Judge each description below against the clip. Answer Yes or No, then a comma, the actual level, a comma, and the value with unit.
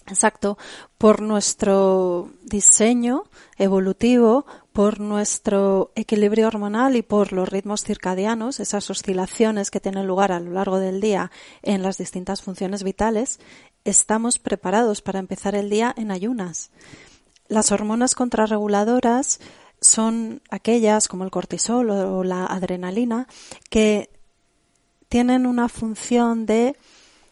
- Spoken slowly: Yes, slow, 115 wpm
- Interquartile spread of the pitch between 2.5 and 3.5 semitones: Yes, average, 2.9 semitones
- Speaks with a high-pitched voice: Yes, high, 210 Hz